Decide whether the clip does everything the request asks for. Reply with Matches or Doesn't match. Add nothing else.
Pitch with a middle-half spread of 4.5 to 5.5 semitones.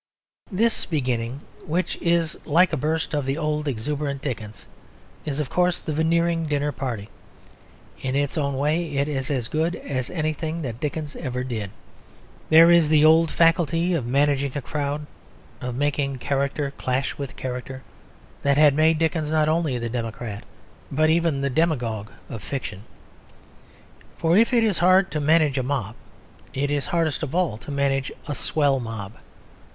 Doesn't match